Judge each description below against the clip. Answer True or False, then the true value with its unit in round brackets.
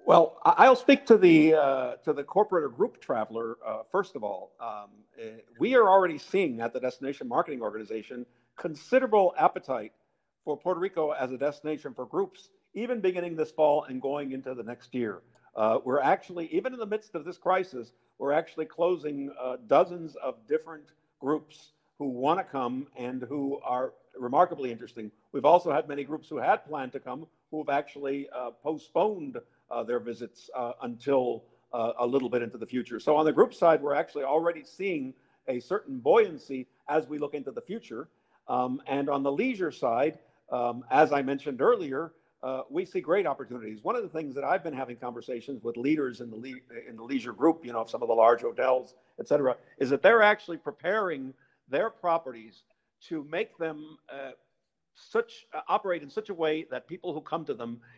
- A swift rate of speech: False (190 wpm)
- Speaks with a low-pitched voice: False (145 Hz)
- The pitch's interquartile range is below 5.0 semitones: False (5.4 semitones)